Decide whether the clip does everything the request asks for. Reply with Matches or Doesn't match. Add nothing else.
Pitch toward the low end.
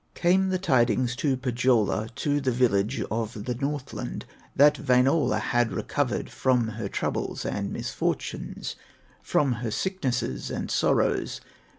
Matches